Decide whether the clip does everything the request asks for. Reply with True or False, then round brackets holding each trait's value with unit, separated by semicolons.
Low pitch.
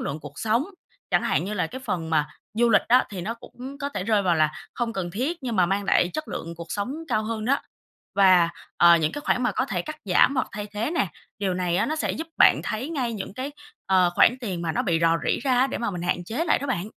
False (210 Hz)